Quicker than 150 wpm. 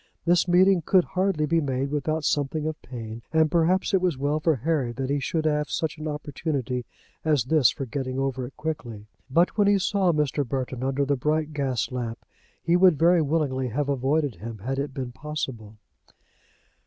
Yes: average, 190 wpm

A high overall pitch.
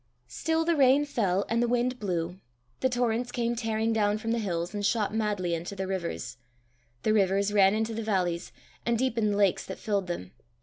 Yes: high, 210 Hz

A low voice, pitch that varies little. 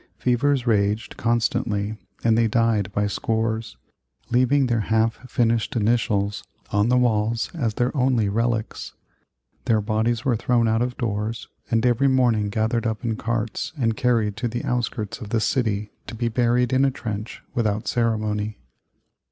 Yes: low, 115 Hz; narrow, 2.1 semitones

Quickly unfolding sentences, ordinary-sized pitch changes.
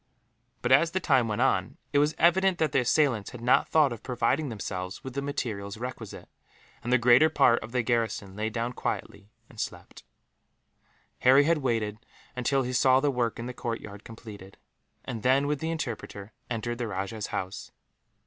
No: average, 180 wpm; average, 3.8 semitones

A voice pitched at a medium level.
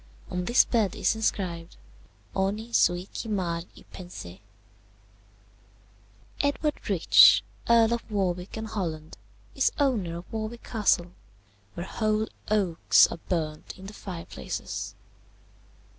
No: high, 195 Hz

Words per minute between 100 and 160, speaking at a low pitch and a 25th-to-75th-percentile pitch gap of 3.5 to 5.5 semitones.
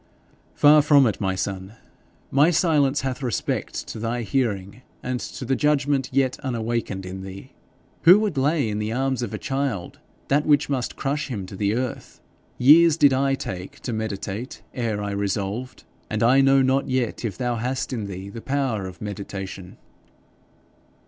No: average, 170 wpm; low, 125 Hz; average, 5.0 semitones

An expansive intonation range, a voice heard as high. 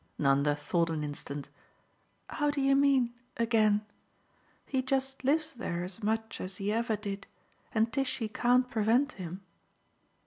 Yes: wide, 5.9 semitones; high, 220 Hz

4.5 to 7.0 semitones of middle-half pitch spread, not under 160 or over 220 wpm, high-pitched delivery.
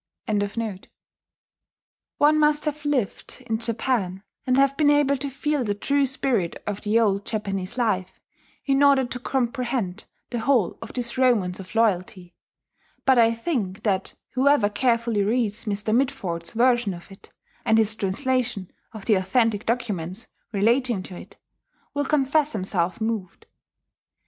No: average, 4.8 semitones; average, 145 wpm; high, 230 Hz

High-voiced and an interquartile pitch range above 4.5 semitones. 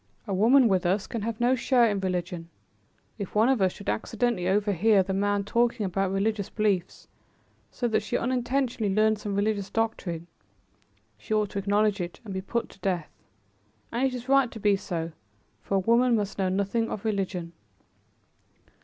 No: high, 205 Hz; average, 3.1 semitones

